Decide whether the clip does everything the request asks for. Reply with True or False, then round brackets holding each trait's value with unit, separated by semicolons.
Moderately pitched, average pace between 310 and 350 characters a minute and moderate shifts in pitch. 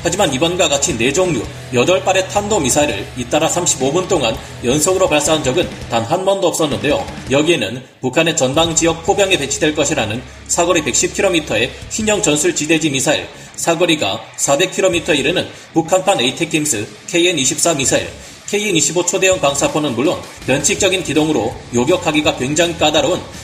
True (165 Hz; 345 characters per minute; 4.7 semitones)